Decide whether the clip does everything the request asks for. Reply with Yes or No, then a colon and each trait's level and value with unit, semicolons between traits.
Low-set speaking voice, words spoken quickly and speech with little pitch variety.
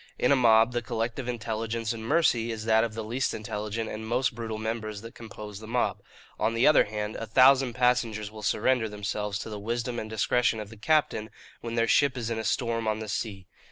Yes: low, 115 Hz; fast, 220 wpm; narrow, 1.8 semitones